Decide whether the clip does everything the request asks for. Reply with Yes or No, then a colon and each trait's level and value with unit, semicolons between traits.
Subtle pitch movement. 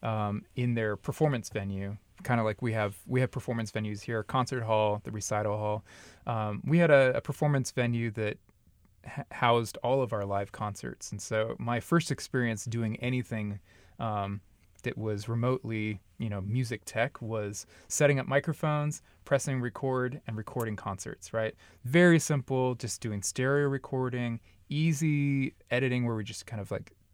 No: average, 3.7 semitones